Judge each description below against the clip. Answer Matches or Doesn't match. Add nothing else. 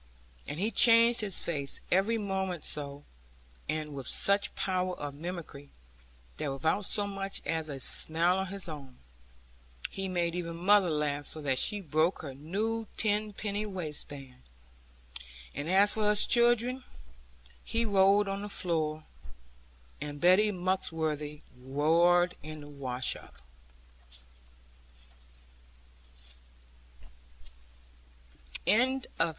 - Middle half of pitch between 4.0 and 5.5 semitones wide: Matches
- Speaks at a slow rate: Matches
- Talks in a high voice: Doesn't match